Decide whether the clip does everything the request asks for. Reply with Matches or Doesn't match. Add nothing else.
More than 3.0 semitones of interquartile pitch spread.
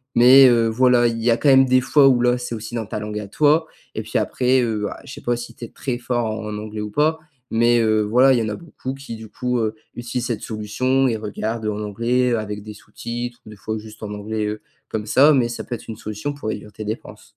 Doesn't match